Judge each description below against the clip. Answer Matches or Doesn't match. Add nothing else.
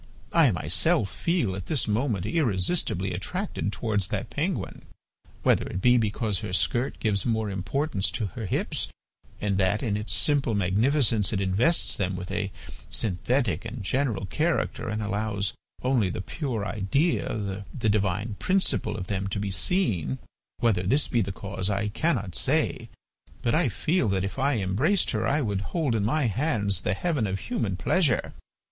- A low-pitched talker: Matches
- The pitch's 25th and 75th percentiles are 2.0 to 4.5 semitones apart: Doesn't match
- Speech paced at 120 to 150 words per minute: Doesn't match